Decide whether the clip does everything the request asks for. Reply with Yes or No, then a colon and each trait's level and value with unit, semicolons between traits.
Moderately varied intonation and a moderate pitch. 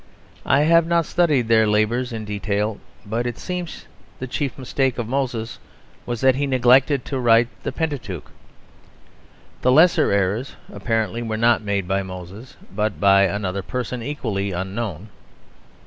No: average, 4.4 semitones; low, 115 Hz